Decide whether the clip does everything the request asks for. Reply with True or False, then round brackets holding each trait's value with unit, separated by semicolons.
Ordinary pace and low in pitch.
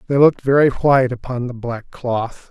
True (190 wpm; 125 Hz)